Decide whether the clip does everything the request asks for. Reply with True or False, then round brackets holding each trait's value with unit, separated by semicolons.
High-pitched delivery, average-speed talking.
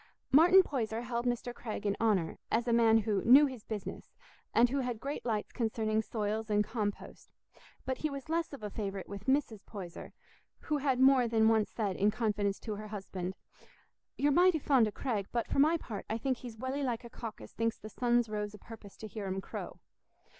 False (225 Hz; 210 wpm)